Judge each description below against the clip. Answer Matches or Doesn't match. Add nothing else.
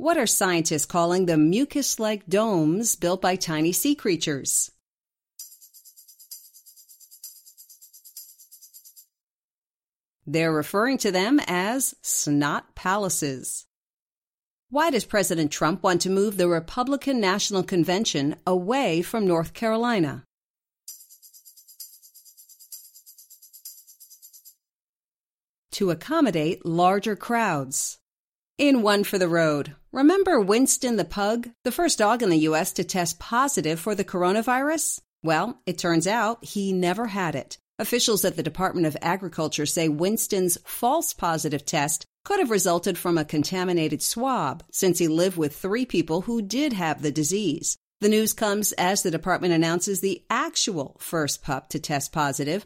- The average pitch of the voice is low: Doesn't match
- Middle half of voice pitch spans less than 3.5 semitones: Doesn't match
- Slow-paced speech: Matches